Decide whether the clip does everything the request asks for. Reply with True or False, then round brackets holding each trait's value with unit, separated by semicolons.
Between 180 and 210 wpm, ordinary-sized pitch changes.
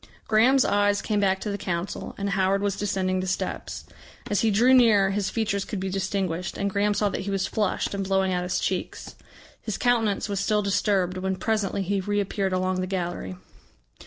False (195 wpm; 1.7 semitones)